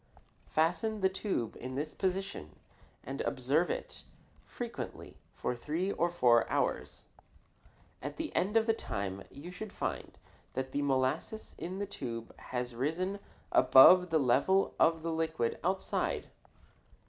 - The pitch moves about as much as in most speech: No, wide, 6.6 semitones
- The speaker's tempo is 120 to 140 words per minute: Yes, slow, 135 wpm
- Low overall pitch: No, medium, 160 Hz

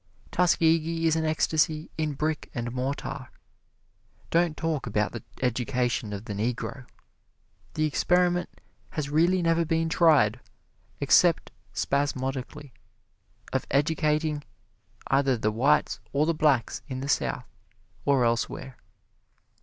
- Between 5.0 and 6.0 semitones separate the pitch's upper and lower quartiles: No, average, 4.1 semitones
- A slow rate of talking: Yes, slow, 115 wpm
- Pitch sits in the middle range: Yes, medium, 145 Hz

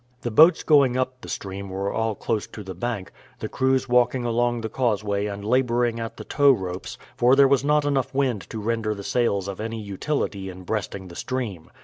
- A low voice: Yes, low, 115 Hz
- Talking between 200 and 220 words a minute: Yes, fast, 205 wpm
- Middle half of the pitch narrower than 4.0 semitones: No, average, 4.3 semitones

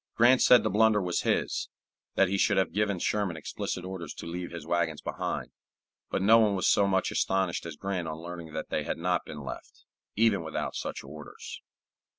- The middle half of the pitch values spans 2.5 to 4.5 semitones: Yes, average, 3.4 semitones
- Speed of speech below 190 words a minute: No, average, 195 wpm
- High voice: No, very low, 90 Hz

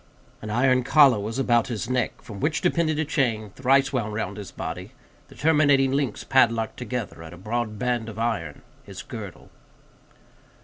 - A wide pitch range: No, average, 3.8 semitones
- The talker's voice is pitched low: Yes, low, 120 Hz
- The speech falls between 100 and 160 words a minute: No, average, 170 wpm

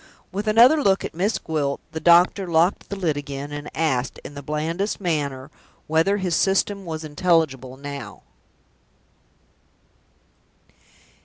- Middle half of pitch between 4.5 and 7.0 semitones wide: Yes, average, 4.9 semitones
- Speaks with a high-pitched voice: No, medium, 160 Hz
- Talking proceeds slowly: Yes, slow, 130 wpm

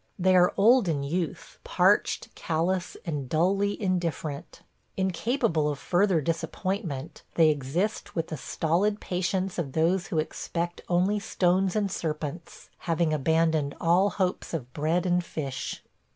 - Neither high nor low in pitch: Yes, medium, 175 Hz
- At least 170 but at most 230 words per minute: No, slow, 135 wpm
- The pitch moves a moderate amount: Yes, average, 3.2 semitones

